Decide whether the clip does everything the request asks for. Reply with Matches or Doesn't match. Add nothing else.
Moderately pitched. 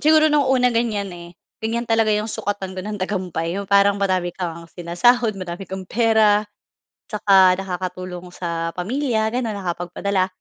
Doesn't match